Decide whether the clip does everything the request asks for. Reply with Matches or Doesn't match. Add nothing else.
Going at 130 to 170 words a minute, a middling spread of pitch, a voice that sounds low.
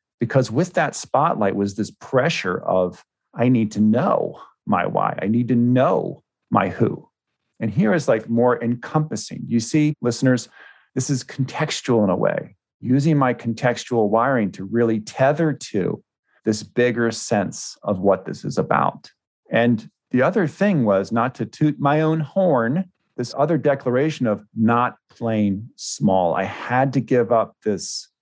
Matches